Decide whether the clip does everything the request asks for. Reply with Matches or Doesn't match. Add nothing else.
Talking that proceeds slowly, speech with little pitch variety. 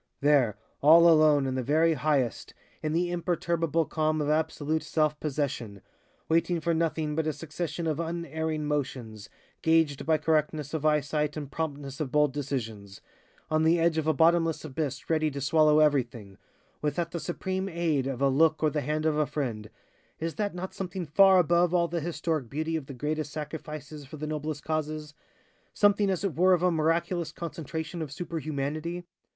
Doesn't match